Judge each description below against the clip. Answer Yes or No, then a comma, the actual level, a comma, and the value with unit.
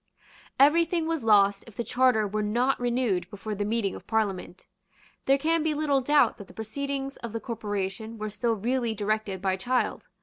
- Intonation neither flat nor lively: Yes, average, 4.6 semitones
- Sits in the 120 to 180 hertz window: No, high, 225 Hz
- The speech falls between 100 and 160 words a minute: No, average, 190 wpm